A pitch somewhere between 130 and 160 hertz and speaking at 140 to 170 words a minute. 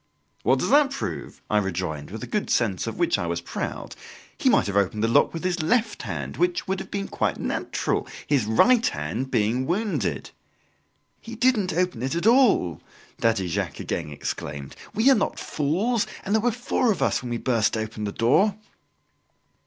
No: medium, 140 Hz; average, 190 wpm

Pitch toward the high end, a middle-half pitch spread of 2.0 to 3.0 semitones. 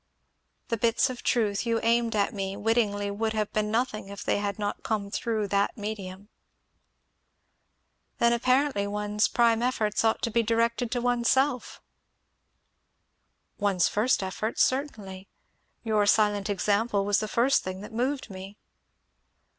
Yes: high, 215 Hz; narrow, 2.5 semitones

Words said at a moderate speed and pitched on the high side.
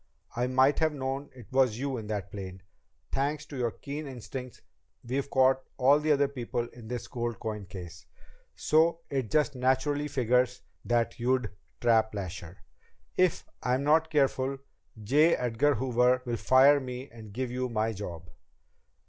No: average, 155 wpm; low, 125 Hz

